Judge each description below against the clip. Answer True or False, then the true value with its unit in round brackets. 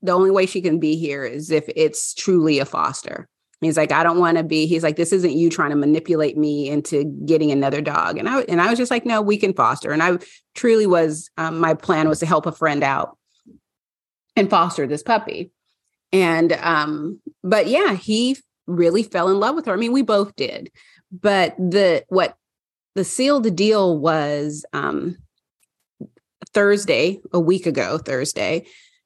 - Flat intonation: False (4.7 semitones)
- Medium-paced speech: True (185 wpm)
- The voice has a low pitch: False (175 Hz)